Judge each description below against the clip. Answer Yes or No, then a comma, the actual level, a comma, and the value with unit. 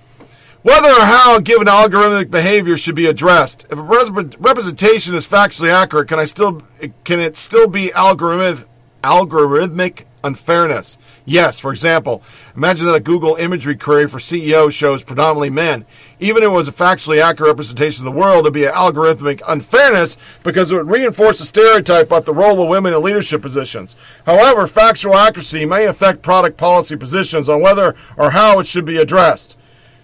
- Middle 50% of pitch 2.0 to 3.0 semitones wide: No, average, 4.7 semitones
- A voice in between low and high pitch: Yes, medium, 165 Hz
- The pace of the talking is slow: No, average, 175 wpm